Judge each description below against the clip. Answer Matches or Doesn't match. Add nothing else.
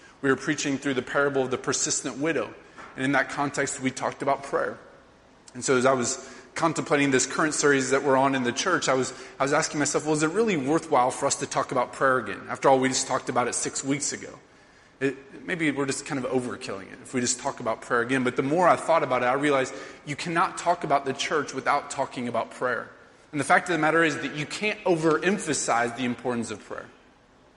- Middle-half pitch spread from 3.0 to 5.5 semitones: Doesn't match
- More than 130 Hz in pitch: Matches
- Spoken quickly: Matches